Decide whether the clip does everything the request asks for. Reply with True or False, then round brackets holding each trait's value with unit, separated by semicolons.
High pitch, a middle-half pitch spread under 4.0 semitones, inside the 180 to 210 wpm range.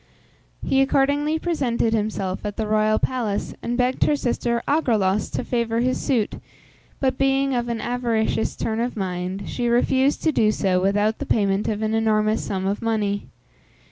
False (225 Hz; 3.5 semitones; 170 wpm)